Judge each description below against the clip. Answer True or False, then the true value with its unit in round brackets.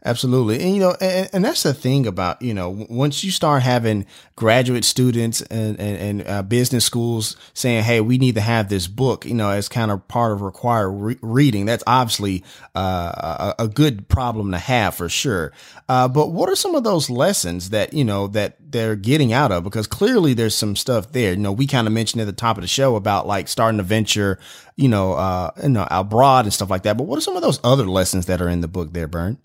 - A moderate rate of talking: False (240 wpm)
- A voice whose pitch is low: True (115 Hz)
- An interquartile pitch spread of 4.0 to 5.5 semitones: True (4.4 semitones)